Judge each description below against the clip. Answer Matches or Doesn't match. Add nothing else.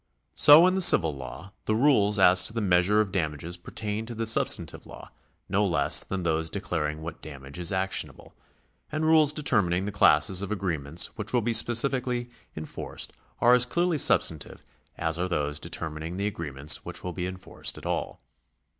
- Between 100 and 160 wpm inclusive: Doesn't match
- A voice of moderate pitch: Doesn't match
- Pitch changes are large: Matches